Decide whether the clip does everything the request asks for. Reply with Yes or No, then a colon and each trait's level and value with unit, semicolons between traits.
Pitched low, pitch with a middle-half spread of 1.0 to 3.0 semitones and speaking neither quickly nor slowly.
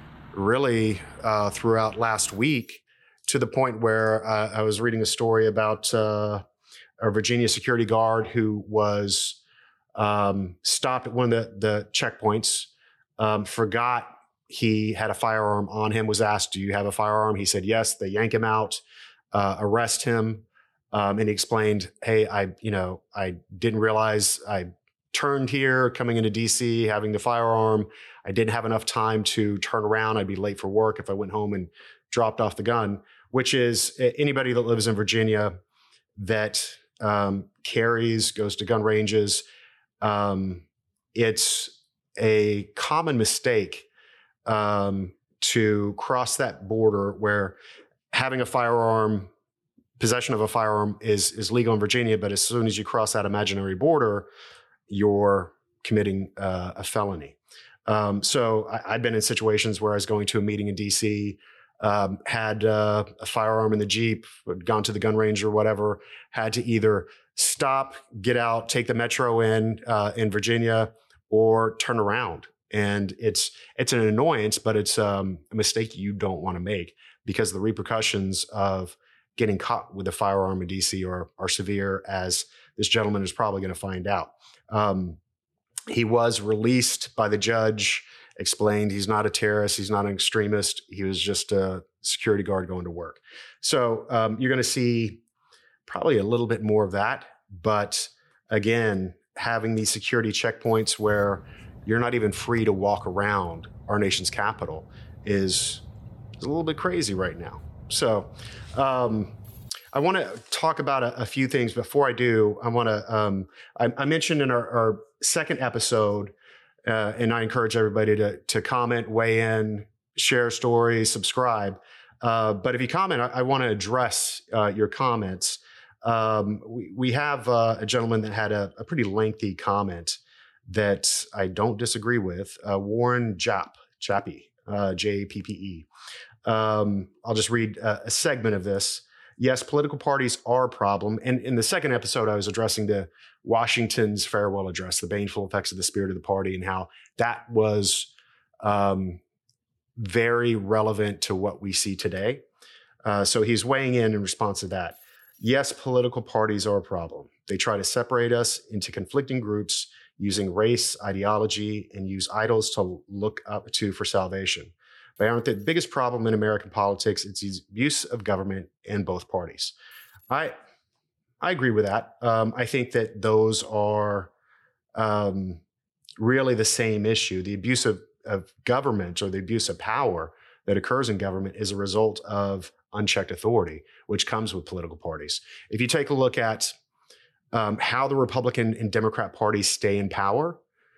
Yes: low, 110 Hz; narrow, 2.4 semitones; average, 165 wpm